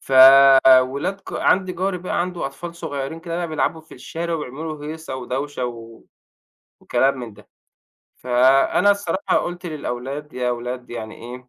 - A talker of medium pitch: Yes, medium, 145 Hz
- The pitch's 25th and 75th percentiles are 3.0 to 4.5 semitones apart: No, average, 5.2 semitones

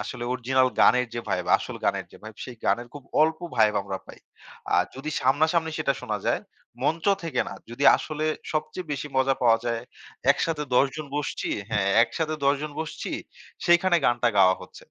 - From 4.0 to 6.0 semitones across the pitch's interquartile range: Yes, average, 4.6 semitones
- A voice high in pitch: No, low, 135 Hz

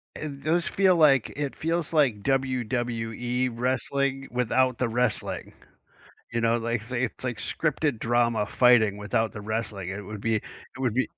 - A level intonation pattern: No, average, 3.2 semitones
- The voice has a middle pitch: No, low, 120 Hz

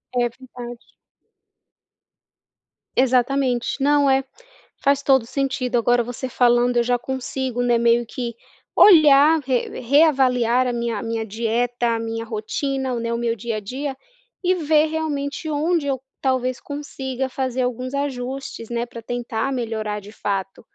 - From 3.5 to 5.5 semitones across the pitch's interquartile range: No, average, 2.7 semitones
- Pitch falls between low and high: No, very high, 250 Hz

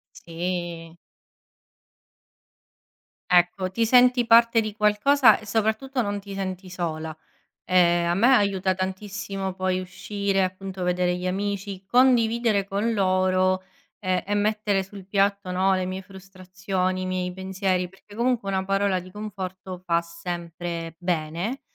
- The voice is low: No, high, 190 Hz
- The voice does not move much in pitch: Yes, narrow, 2.1 semitones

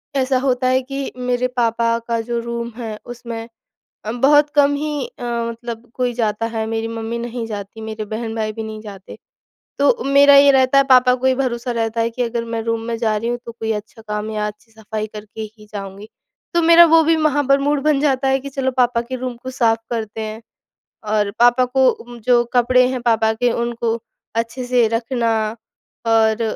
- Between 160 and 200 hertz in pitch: No, high, 235 Hz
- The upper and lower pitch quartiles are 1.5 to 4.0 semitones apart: Yes, narrow, 2.4 semitones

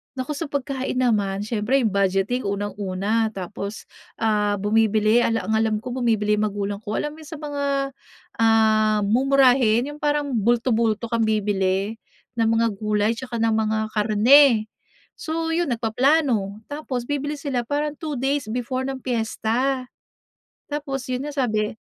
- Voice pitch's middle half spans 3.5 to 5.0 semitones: Yes, average, 4.2 semitones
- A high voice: Yes, high, 230 Hz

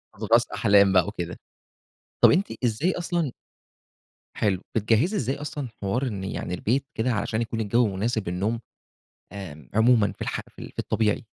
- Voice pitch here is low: Yes, low, 110 Hz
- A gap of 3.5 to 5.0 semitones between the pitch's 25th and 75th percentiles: Yes, average, 4.1 semitones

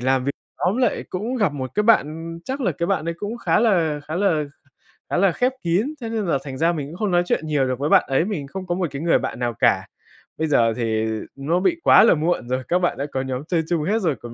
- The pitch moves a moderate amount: No, wide, 5.9 semitones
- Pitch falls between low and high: Yes, medium, 165 Hz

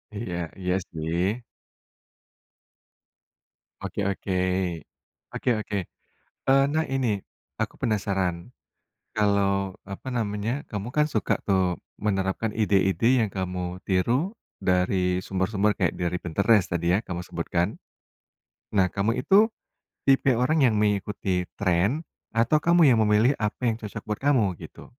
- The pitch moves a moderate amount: Yes, average, 4.0 semitones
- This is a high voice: No, low, 100 Hz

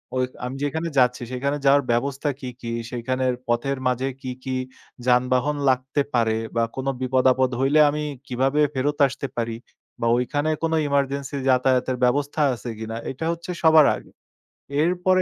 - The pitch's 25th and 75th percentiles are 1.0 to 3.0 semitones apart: Yes, narrow, 2.4 semitones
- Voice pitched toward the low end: Yes, low, 130 Hz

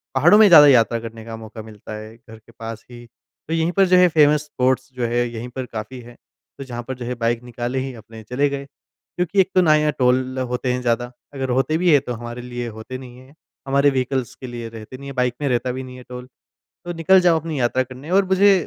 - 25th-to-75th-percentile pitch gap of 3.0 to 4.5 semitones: Yes, average, 3.3 semitones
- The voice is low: Yes, low, 125 Hz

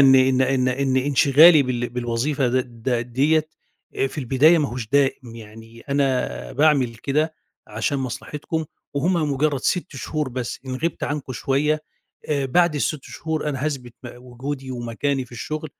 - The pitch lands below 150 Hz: Yes, low, 135 Hz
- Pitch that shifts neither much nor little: Yes, average, 3.3 semitones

